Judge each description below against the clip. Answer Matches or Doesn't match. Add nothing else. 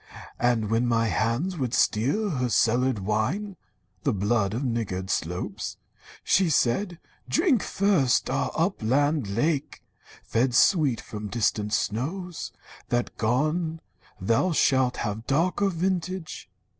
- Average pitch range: Doesn't match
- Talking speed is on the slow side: Matches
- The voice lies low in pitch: Matches